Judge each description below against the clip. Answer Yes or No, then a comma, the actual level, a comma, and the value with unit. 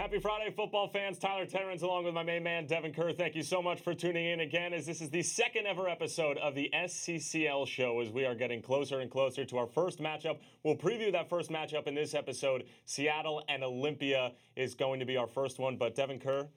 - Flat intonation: No, average, 4.4 semitones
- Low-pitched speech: No, medium, 155 Hz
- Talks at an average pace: No, fast, 230 wpm